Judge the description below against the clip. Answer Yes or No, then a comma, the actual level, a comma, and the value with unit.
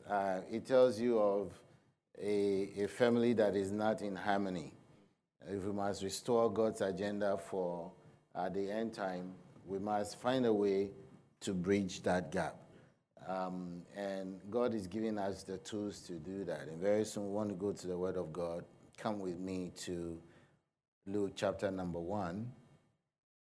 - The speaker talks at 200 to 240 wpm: No, average, 165 wpm